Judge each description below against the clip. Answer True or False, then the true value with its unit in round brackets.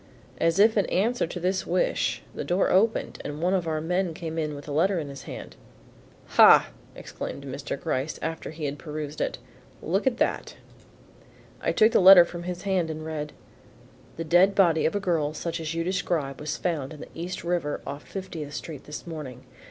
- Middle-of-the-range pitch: True (165 Hz)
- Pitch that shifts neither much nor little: True (3.3 semitones)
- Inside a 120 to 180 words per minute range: False (200 wpm)